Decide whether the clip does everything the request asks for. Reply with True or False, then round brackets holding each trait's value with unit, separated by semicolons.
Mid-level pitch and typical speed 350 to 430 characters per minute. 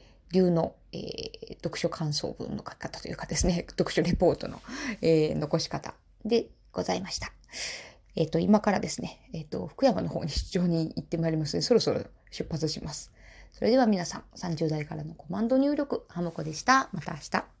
True (175 Hz; 360 characters per minute)